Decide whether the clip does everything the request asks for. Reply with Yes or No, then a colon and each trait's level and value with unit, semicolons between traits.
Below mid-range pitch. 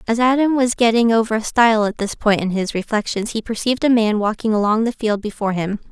No: high, 220 Hz